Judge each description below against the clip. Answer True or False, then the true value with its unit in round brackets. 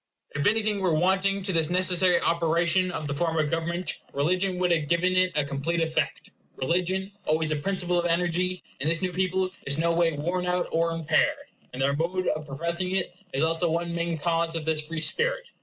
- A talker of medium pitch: True (170 Hz)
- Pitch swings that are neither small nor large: False (2.3 semitones)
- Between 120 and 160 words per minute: False (205 wpm)